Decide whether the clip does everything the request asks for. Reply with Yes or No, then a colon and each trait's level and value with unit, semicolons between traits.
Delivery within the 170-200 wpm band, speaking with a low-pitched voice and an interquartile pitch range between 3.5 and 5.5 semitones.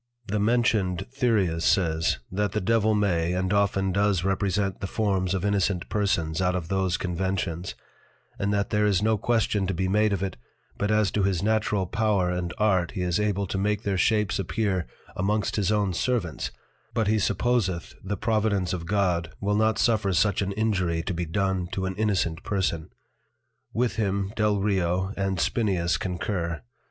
No: average, 175 wpm; very low, 95 Hz; narrow, 2.6 semitones